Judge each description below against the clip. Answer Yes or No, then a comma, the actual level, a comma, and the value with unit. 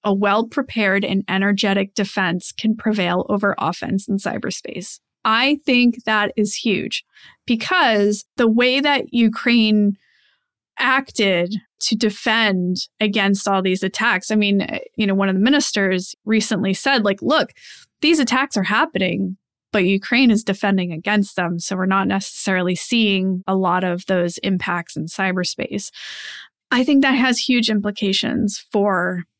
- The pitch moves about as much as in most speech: Yes, average, 3.0 semitones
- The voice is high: Yes, high, 205 Hz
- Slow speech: No, average, 145 wpm